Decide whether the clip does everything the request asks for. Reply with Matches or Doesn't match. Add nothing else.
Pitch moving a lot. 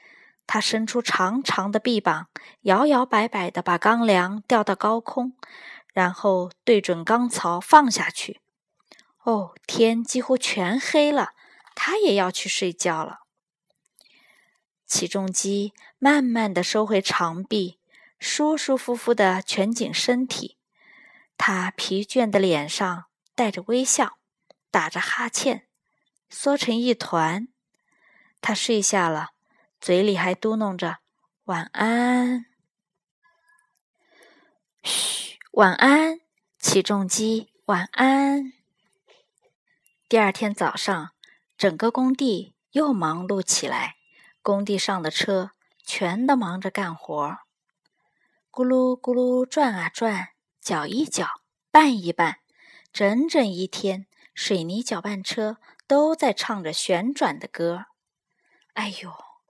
Doesn't match